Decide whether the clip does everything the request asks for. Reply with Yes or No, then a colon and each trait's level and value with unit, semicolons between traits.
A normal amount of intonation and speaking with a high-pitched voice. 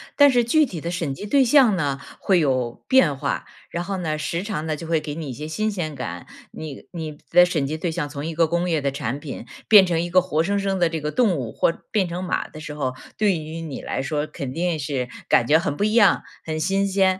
No: average, 4.3 semitones; medium, 165 Hz